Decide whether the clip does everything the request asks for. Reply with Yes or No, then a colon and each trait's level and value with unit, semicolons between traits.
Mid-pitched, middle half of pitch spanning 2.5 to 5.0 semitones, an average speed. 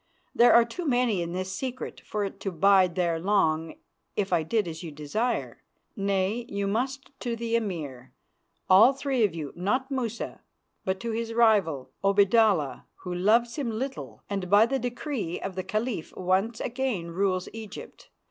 No: high, 200 Hz; average, 4.5 semitones; average, 165 wpm